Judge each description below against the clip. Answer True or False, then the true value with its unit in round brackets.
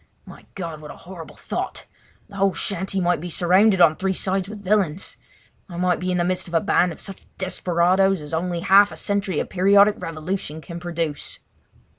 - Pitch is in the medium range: True (180 Hz)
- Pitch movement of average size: False (2.3 semitones)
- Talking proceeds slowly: False (195 wpm)